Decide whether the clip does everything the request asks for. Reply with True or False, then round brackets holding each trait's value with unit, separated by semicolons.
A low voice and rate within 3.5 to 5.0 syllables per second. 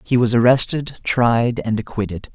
True (120 Hz; 4.5 syllables/s)